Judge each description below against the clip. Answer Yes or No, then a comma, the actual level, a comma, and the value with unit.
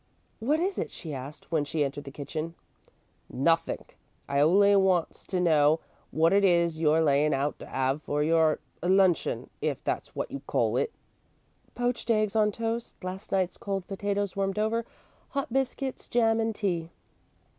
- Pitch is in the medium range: Yes, medium, 180 Hz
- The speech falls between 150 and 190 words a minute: Yes, average, 165 wpm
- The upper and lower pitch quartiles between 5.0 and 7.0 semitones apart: Yes, wide, 5.5 semitones